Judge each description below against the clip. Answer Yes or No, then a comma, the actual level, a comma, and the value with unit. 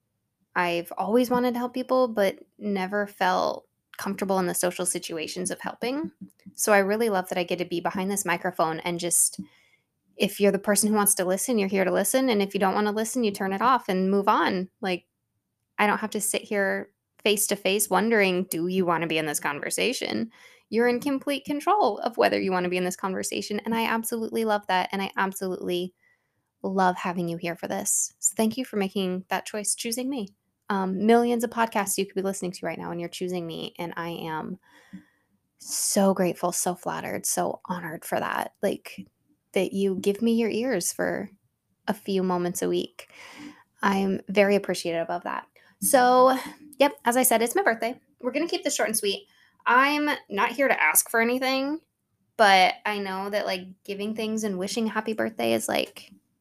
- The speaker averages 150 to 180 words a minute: No, average, 200 wpm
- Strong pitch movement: No, average, 4.0 semitones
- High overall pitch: Yes, high, 195 Hz